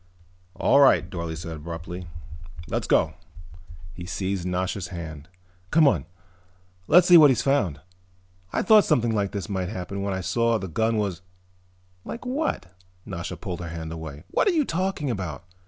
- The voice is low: Yes, very low, 95 Hz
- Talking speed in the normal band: Yes, average, 170 wpm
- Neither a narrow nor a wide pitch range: No, wide, 6.2 semitones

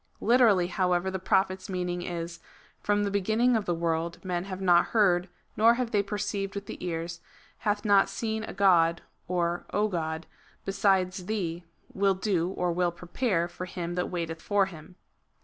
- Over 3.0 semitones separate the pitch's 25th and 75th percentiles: No, narrow, 2.6 semitones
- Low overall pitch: No, medium, 185 Hz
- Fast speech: No, average, 165 wpm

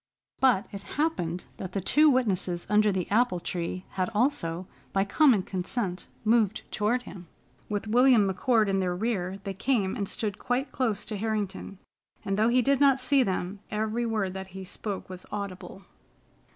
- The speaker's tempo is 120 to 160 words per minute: No, average, 170 wpm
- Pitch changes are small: No, average, 4.1 semitones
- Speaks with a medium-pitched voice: No, high, 205 Hz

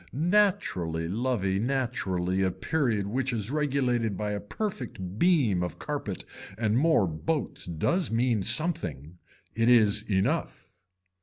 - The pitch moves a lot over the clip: Yes, wide, 6.2 semitones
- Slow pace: Yes, slow, 125 wpm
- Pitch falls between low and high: No, low, 110 Hz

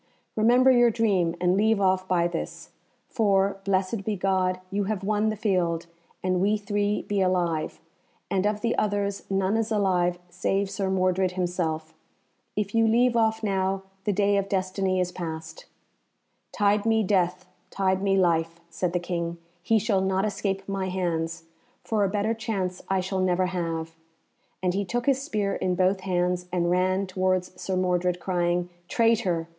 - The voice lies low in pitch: No, high, 190 Hz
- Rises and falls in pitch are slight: Yes, narrow, 2.3 semitones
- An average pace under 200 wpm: Yes, average, 165 wpm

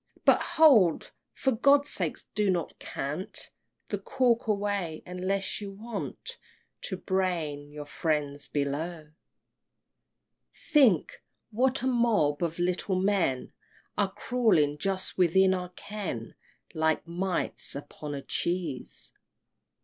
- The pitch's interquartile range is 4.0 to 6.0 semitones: Yes, average, 5.1 semitones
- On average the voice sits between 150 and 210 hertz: Yes, medium, 185 Hz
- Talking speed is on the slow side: Yes, slow, 115 wpm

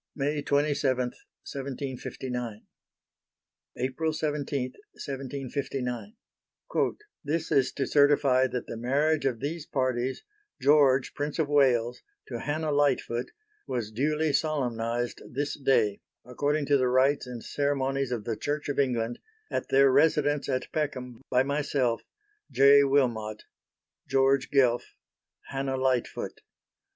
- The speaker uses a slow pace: Yes, slow, 115 wpm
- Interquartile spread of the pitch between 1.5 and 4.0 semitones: Yes, narrow, 2.5 semitones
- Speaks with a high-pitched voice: No, low, 135 Hz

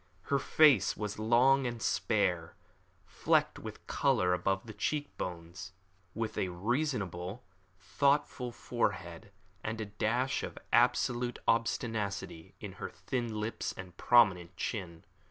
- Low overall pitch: Yes, low, 110 Hz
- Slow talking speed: Yes, slow, 120 wpm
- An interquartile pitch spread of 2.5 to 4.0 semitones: No, average, 4.7 semitones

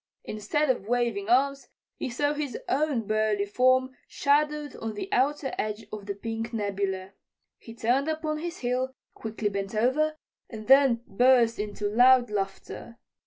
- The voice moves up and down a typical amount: Yes, average, 4.4 semitones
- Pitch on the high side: Yes, high, 240 Hz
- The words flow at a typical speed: Yes, average, 150 wpm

